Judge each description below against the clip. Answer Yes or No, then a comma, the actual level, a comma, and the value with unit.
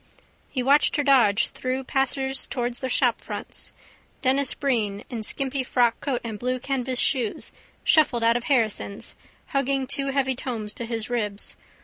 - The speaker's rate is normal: Yes, average, 145 wpm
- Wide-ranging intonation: No, narrow, 2.6 semitones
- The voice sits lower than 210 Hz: No, very high, 255 Hz